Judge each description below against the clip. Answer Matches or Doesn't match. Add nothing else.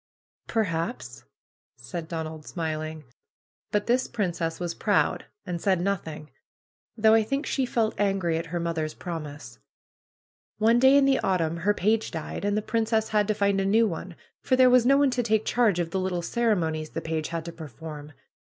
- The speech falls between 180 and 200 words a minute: Matches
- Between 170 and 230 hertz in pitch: Matches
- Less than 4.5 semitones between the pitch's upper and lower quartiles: Doesn't match